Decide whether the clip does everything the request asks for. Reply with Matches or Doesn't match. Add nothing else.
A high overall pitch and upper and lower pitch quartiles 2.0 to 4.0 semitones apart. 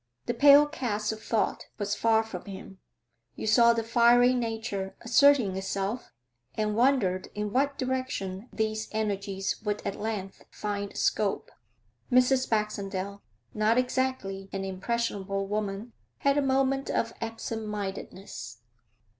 Matches